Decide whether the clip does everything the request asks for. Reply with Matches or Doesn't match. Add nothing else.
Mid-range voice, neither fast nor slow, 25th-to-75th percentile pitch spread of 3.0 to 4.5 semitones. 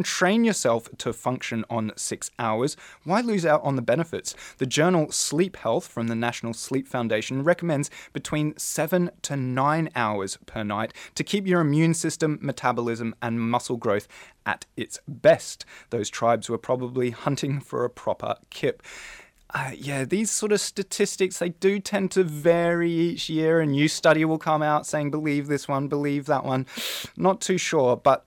Doesn't match